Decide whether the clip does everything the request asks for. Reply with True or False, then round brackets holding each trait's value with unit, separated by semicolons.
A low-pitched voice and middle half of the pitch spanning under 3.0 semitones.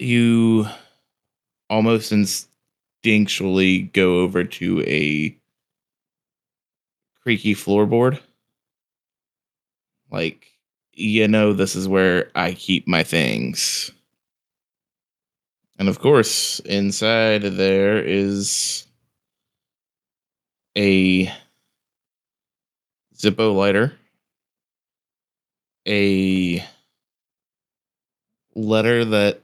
True (100 Hz; 2.4 semitones)